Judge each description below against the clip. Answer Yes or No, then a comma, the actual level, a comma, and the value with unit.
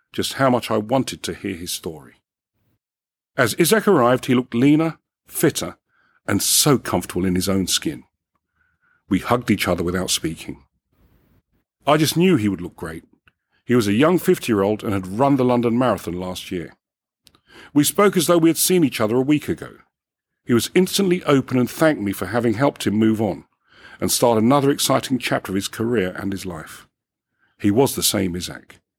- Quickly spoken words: No, average, 190 wpm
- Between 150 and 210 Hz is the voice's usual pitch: No, low, 120 Hz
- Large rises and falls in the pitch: Yes, wide, 7.0 semitones